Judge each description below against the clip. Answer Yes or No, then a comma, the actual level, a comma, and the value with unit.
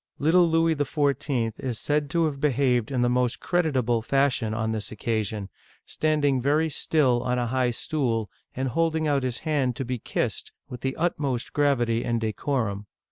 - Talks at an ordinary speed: Yes, average, 170 wpm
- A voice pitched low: Yes, low, 130 Hz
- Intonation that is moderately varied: Yes, average, 3.8 semitones